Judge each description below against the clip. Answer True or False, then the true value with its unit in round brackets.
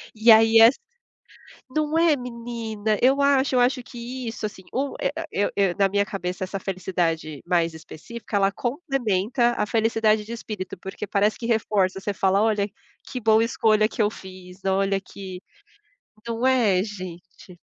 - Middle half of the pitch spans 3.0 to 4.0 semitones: True (3.6 semitones)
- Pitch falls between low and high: False (215 Hz)